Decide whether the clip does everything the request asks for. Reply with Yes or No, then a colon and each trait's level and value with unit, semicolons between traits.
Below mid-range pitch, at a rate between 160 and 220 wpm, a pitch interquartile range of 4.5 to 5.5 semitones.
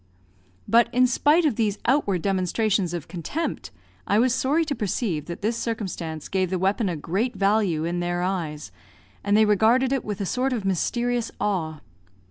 No: high, 205 Hz; average, 175 wpm; average, 5.2 semitones